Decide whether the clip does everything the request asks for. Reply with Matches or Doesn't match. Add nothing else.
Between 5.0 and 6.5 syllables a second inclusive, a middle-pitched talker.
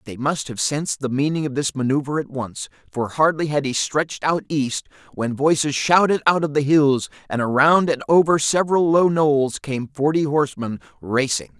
Matches